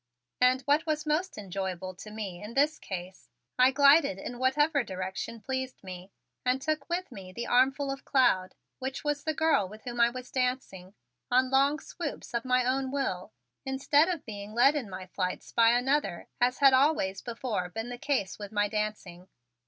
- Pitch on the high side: Yes, very high, 250 Hz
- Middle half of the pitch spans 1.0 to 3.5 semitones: No, wide, 5.6 semitones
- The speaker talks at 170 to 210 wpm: Yes, average, 185 wpm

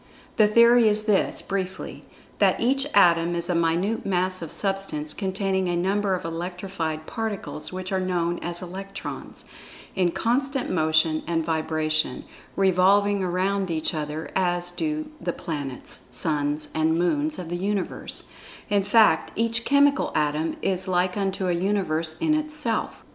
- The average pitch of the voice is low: No, medium, 185 Hz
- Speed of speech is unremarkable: Yes, average, 145 wpm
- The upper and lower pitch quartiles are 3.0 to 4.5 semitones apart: Yes, average, 3.6 semitones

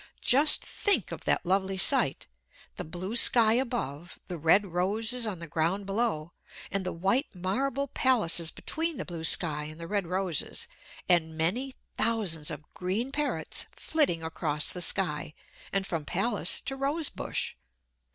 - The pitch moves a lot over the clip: Yes, wide, 6.2 semitones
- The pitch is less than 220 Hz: Yes, high, 190 Hz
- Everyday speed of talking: Yes, average, 150 wpm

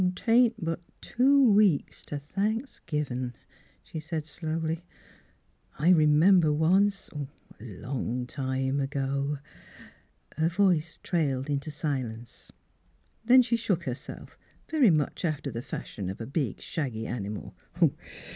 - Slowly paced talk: Yes, slow, 130 wpm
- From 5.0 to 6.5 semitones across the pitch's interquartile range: Yes, wide, 5.5 semitones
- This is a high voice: No, medium, 155 Hz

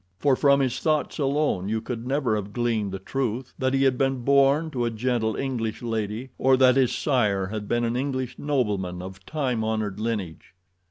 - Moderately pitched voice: No, low, 120 Hz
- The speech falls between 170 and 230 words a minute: Yes, average, 195 wpm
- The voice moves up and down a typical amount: Yes, average, 3.8 semitones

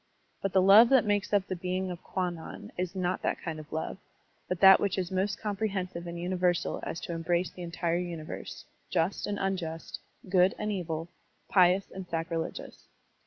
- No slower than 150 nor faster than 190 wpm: Yes, average, 180 wpm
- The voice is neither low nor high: Yes, medium, 180 Hz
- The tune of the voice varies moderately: No, narrow, 2.1 semitones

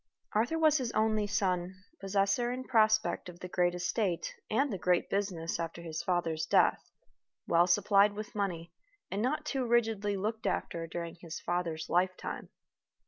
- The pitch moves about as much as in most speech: Yes, average, 3.8 semitones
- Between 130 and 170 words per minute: Yes, average, 155 wpm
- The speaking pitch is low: No, high, 195 Hz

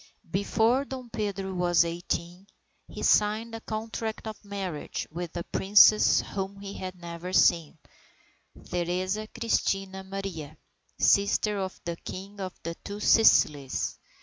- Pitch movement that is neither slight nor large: Yes, average, 3.1 semitones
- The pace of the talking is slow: Yes, slow, 125 wpm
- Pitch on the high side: Yes, high, 195 Hz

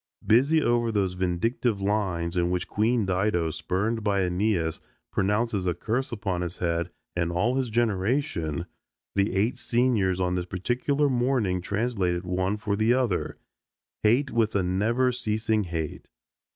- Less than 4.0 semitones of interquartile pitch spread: No, average, 4.6 semitones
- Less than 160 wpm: Yes, average, 145 wpm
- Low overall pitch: Yes, low, 100 Hz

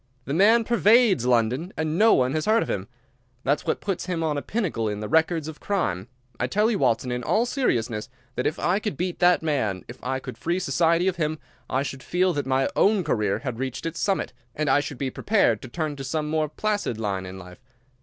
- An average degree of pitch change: No, wide, 6.6 semitones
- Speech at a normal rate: No, fast, 230 wpm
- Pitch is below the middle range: No, medium, 150 Hz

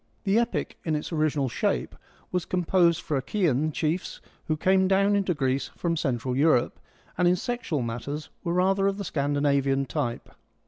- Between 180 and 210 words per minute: No, average, 170 wpm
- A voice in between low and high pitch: Yes, medium, 155 Hz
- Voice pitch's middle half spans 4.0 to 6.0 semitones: Yes, average, 5.0 semitones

